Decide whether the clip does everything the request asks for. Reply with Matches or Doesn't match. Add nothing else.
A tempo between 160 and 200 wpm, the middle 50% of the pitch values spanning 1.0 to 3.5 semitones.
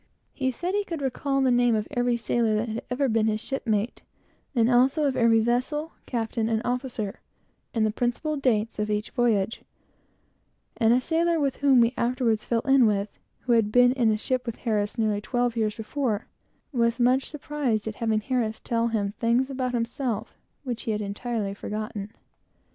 Matches